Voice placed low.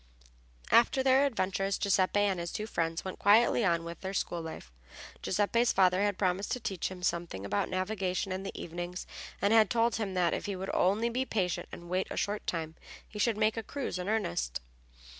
No: high, 190 Hz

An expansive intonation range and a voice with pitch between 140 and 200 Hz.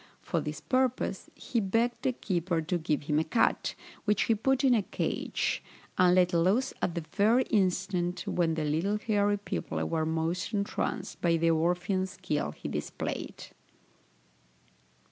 No: average, 4.1 semitones; medium, 185 Hz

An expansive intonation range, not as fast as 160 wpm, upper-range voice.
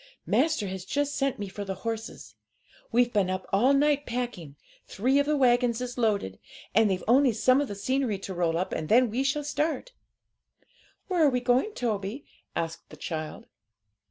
No: wide, 5.8 semitones; average, 185 wpm; high, 240 Hz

